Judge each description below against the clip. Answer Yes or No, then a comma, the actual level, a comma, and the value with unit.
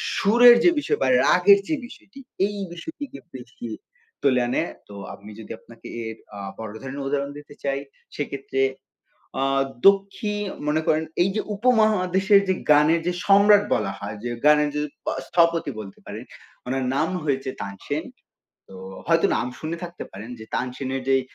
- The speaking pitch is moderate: Yes, medium, 150 Hz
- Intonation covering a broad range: Yes, wide, 7.0 semitones